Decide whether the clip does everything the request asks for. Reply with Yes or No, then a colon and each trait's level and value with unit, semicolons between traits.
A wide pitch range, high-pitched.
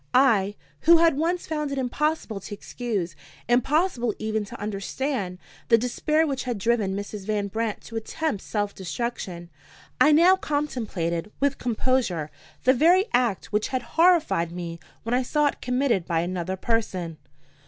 Yes: wide, 6.2 semitones; high, 235 Hz